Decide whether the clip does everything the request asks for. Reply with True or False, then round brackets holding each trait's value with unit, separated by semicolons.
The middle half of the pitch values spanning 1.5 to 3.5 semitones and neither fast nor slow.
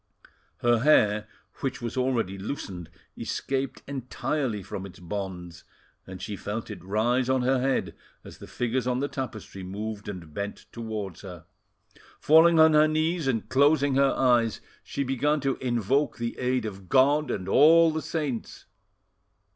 False (5.2 semitones; 155 wpm)